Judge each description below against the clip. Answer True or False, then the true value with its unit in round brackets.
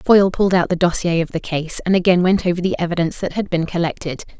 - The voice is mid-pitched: True (175 Hz)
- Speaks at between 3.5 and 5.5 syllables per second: False (6.9 syllables/s)